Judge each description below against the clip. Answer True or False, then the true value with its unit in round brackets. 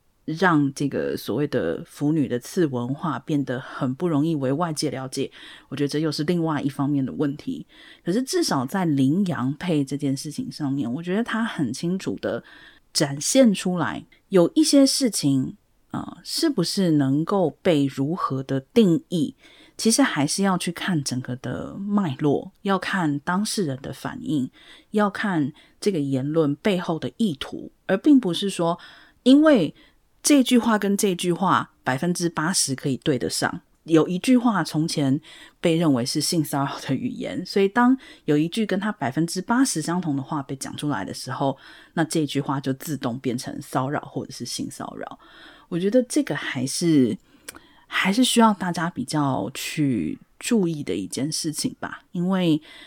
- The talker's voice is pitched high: False (160 Hz)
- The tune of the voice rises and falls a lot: True (6.3 semitones)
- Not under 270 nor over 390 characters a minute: False (250 characters per minute)